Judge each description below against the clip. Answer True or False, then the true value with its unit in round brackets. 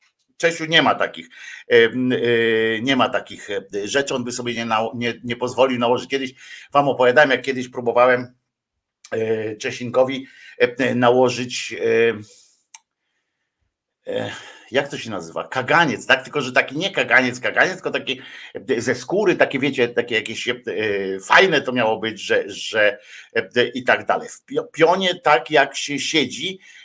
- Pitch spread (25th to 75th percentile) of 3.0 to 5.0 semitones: True (3.4 semitones)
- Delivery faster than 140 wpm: False (130 wpm)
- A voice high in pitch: False (125 Hz)